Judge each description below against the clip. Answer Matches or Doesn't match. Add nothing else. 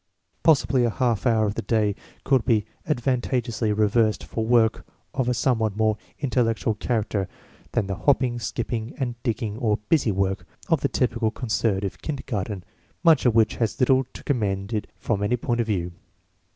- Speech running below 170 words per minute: Doesn't match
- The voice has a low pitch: Matches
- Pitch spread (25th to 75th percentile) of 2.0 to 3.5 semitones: Matches